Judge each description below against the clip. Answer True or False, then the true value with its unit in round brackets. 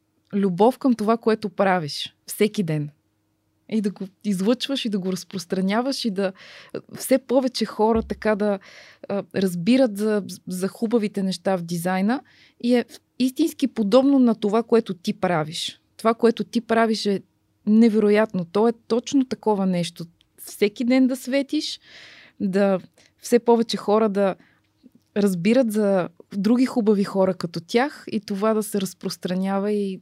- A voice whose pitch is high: True (210 Hz)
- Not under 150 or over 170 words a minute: False (140 wpm)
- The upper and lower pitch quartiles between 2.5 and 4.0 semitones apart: True (3.5 semitones)